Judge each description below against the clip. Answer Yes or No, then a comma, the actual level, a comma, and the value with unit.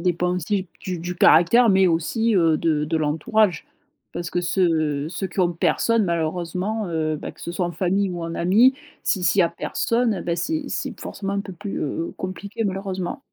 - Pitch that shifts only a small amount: No, average, 3.0 semitones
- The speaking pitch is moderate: Yes, medium, 180 Hz